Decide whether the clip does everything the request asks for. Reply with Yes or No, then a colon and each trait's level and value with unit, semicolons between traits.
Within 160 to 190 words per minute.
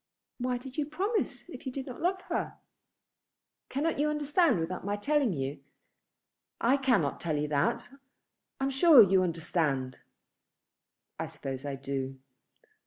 No: average, 145 wpm